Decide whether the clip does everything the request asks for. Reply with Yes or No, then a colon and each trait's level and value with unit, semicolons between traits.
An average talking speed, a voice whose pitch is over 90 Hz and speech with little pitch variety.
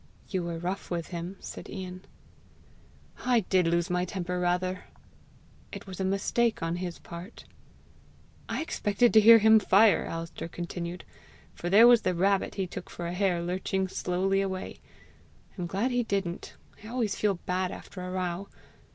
Yes: average, 165 wpm; medium, 185 Hz; narrow, 2.3 semitones